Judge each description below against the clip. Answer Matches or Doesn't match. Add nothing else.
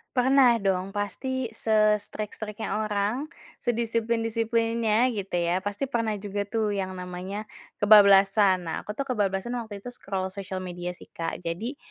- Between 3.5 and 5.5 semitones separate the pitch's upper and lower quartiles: Doesn't match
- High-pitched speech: Matches